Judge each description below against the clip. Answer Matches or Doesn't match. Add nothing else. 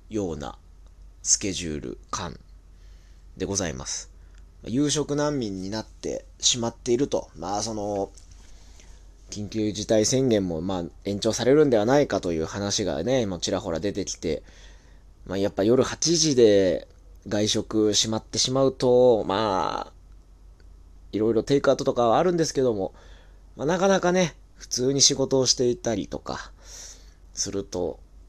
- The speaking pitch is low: Matches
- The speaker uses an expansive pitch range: Matches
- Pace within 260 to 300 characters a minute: Matches